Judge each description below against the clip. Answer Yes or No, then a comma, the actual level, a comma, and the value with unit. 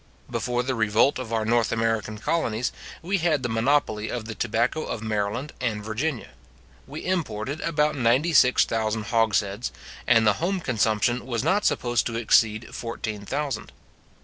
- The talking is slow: No, average, 155 wpm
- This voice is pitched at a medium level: No, low, 115 Hz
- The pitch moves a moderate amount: Yes, average, 4.2 semitones